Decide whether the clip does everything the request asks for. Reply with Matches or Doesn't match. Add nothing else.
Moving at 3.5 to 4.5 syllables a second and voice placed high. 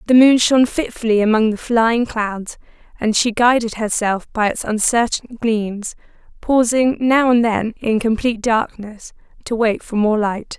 Matches